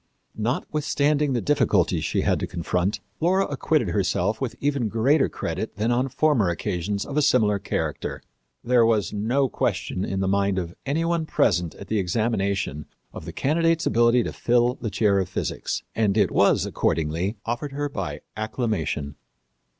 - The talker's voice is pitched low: Yes, low, 110 Hz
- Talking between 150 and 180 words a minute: Yes, average, 165 wpm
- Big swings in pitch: Yes, wide, 6.1 semitones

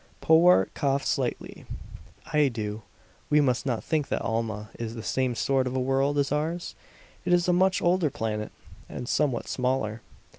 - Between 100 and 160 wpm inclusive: No, average, 170 wpm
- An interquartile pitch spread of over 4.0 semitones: Yes, average, 4.8 semitones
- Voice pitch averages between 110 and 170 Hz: Yes, low, 135 Hz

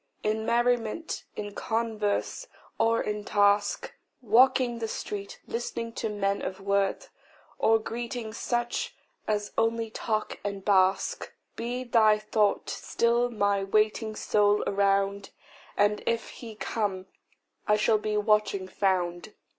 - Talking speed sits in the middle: No, slow, 125 wpm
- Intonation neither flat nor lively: No, narrow, 2.3 semitones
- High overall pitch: Yes, high, 215 Hz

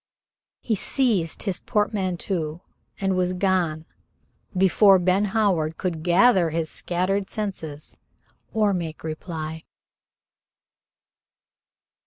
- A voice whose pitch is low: No, medium, 185 Hz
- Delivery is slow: Yes, slow, 90 wpm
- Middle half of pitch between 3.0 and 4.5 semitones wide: Yes, average, 3.4 semitones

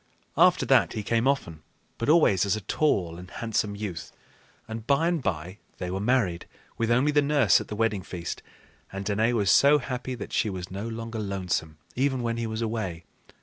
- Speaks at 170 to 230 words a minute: Yes, average, 195 wpm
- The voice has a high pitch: No, low, 110 Hz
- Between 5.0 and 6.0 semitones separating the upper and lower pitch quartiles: No, average, 4.4 semitones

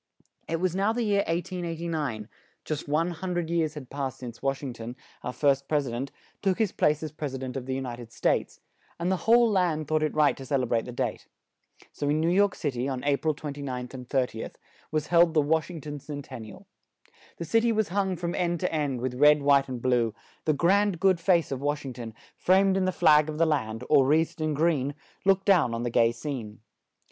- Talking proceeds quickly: Yes, fast, 240 wpm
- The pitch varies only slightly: No, average, 4.7 semitones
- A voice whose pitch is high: No, medium, 150 Hz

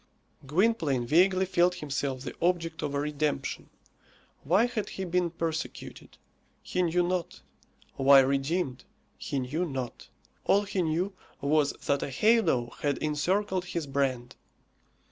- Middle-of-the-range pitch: Yes, medium, 160 Hz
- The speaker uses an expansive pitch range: No, average, 4.5 semitones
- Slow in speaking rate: Yes, slow, 130 wpm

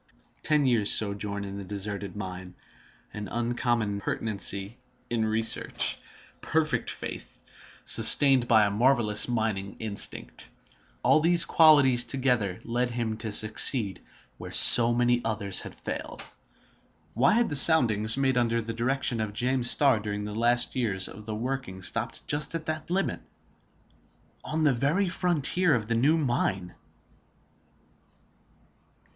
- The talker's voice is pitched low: Yes, low, 115 Hz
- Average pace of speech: No, slow, 130 wpm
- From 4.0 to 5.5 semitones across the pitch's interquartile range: Yes, average, 4.5 semitones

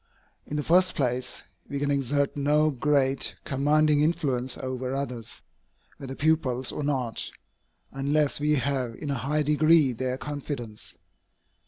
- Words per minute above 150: No, slow, 135 wpm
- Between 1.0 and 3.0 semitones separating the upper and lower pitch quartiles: Yes, narrow, 2.5 semitones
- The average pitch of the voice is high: No, medium, 140 Hz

